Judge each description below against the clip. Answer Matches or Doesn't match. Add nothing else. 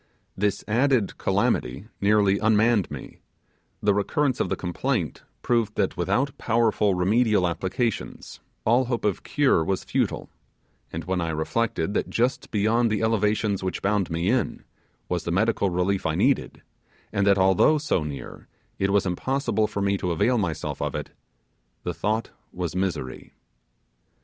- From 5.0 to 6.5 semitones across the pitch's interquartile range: Doesn't match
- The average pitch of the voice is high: Doesn't match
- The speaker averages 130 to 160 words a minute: Matches